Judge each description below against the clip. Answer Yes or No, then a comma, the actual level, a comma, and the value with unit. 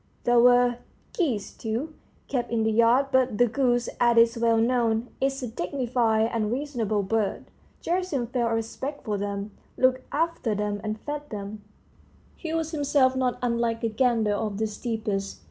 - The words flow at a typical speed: Yes, average, 165 wpm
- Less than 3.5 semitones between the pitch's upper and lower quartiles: Yes, average, 3.0 semitones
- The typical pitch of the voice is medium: No, high, 235 Hz